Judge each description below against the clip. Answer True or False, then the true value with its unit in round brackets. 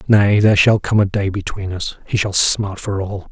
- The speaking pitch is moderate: False (100 Hz)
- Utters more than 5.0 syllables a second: False (4.9 syllables/s)